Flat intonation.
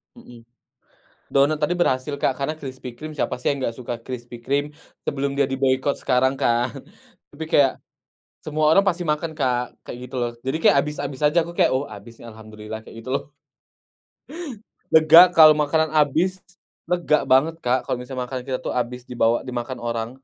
No: average, 3.6 semitones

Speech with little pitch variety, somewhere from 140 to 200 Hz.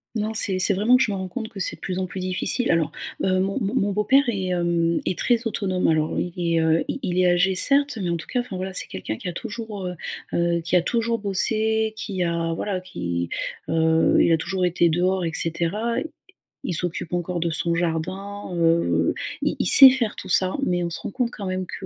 No: average, 3.5 semitones; medium, 185 Hz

